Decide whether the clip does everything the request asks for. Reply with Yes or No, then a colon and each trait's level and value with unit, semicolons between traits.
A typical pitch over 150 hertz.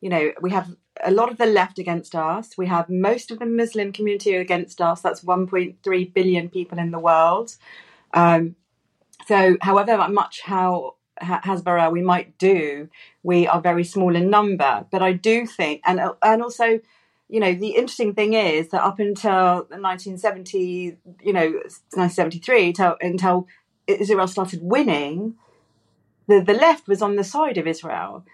Yes: medium, 185 Hz